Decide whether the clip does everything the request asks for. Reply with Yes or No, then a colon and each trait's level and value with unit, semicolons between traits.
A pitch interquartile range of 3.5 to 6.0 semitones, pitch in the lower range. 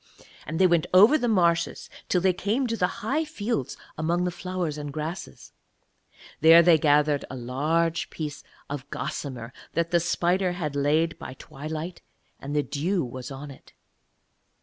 No: average, 3.9 semitones; medium, 165 Hz